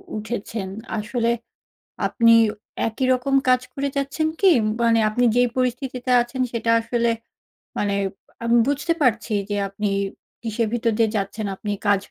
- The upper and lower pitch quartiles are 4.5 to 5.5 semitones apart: No, narrow, 2.5 semitones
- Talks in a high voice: Yes, high, 235 Hz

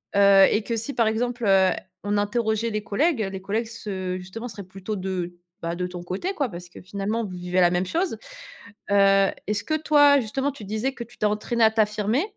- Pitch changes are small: No, average, 3.6 semitones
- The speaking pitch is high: Yes, high, 210 Hz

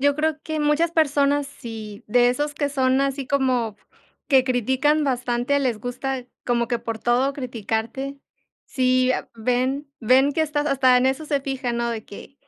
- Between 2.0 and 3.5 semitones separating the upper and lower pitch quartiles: Yes, average, 2.7 semitones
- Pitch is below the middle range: No, very high, 265 Hz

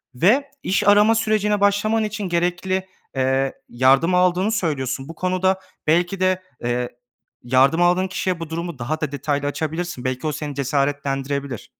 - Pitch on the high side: No, medium, 170 Hz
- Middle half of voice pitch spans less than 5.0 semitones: No, wide, 5.4 semitones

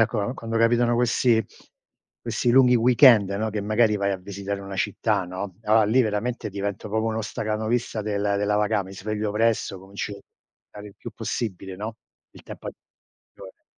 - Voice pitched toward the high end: No, low, 105 Hz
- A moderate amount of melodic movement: No, narrow, 2.3 semitones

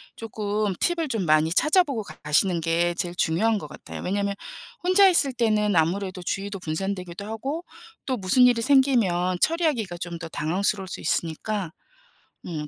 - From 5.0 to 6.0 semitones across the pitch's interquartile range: Yes, average, 5.3 semitones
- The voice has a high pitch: Yes, high, 200 Hz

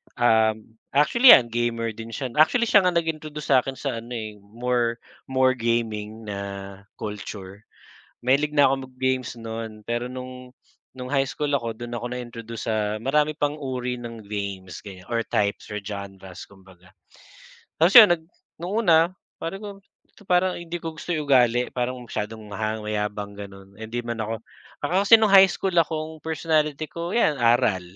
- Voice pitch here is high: No, low, 120 Hz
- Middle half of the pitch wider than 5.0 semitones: Yes, wide, 5.6 semitones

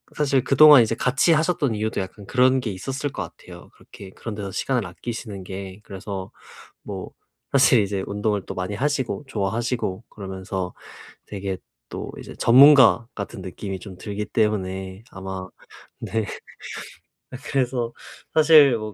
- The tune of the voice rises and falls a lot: No, average, 5.0 semitones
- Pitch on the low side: Yes, low, 110 Hz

